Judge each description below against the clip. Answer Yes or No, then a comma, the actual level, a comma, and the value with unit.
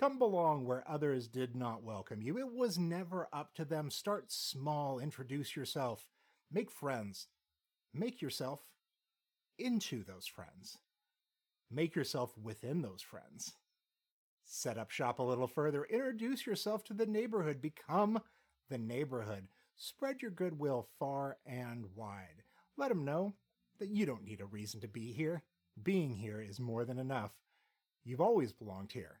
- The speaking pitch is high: No, medium, 140 Hz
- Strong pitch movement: Yes, wide, 7.0 semitones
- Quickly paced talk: No, average, 150 wpm